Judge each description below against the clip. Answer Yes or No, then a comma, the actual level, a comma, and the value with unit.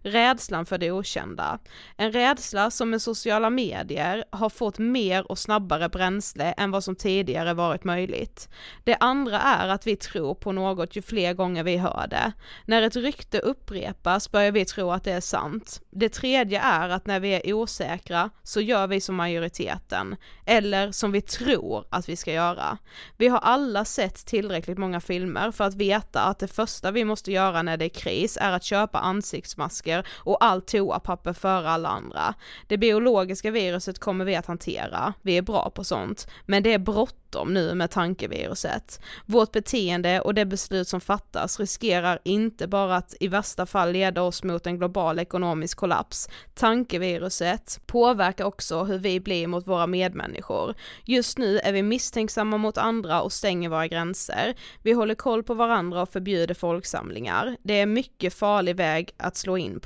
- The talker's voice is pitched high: Yes, high, 195 Hz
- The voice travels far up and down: No, average, 3.4 semitones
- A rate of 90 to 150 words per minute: No, average, 175 wpm